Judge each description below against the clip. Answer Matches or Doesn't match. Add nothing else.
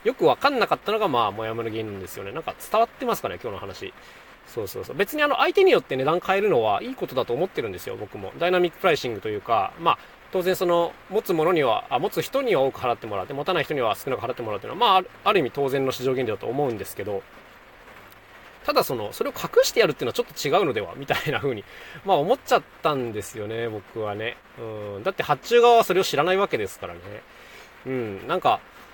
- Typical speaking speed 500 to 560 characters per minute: Matches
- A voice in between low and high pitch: Matches